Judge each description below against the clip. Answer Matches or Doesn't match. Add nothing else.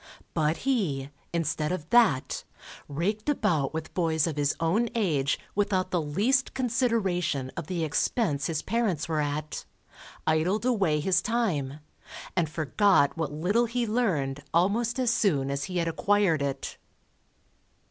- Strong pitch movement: Matches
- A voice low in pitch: Doesn't match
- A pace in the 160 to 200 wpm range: Doesn't match